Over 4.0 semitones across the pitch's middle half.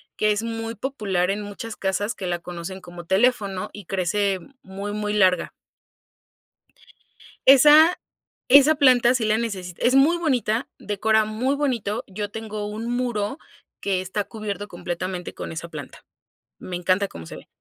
No: average, 3.7 semitones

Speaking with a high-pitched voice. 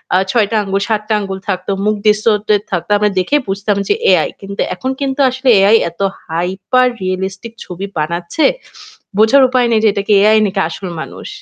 Yes: high, 205 Hz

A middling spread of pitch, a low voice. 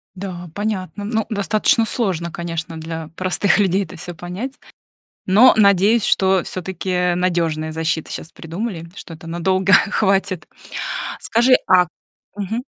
No: average, 3.1 semitones; medium, 185 Hz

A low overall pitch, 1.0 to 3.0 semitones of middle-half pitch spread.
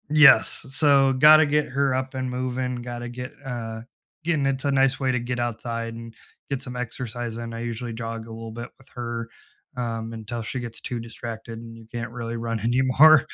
Yes: low, 120 Hz; narrow, 2.4 semitones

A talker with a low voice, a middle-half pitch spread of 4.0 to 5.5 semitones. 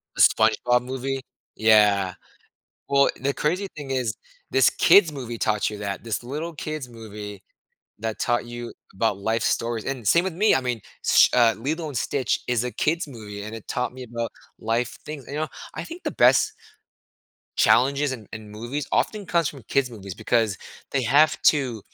Yes: low, 125 Hz; average, 4.3 semitones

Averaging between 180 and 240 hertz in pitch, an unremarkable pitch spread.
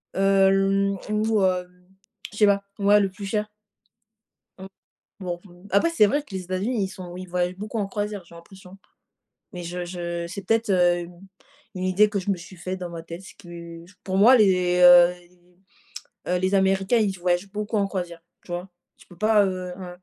No: high, 190 Hz; narrow, 2.2 semitones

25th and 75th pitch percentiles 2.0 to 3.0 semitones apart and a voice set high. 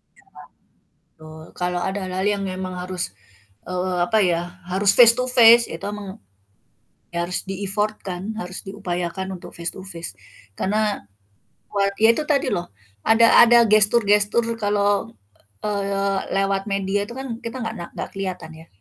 Yes: average, 2.7 semitones; high, 195 Hz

